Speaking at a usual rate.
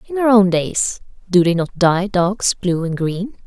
No: fast, 210 wpm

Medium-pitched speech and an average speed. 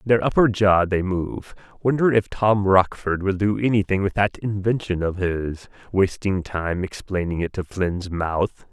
No: very low, 95 Hz; average, 165 wpm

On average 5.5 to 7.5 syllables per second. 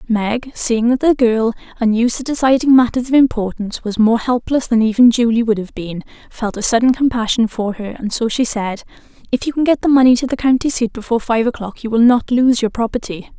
Yes: 5.7 syllables/s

